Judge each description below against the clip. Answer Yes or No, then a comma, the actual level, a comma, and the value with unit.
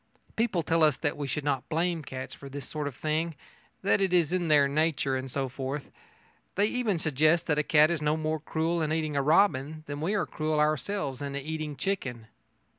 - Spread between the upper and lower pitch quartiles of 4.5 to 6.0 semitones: No, average, 2.8 semitones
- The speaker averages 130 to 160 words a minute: No, average, 200 wpm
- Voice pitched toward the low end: No, medium, 155 Hz